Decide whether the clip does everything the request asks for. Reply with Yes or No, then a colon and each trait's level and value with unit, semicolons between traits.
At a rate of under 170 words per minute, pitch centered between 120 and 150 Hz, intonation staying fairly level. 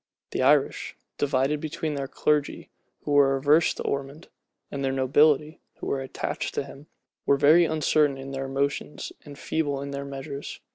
No: average, 175 wpm; medium, 140 Hz; narrow, 1.6 semitones